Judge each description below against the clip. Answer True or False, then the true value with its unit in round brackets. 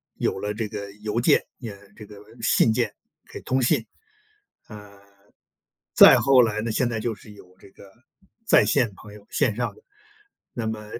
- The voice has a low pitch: True (110 Hz)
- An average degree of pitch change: False (2.1 semitones)